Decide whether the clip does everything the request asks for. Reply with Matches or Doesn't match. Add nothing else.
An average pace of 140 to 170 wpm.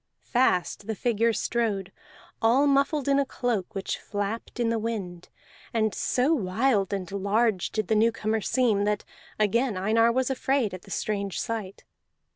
Matches